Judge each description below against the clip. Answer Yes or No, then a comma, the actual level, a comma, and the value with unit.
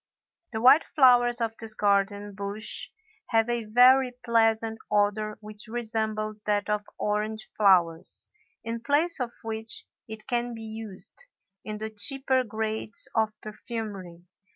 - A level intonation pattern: Yes, narrow, 2.1 semitones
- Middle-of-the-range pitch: No, high, 220 Hz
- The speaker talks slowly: Yes, slow, 130 wpm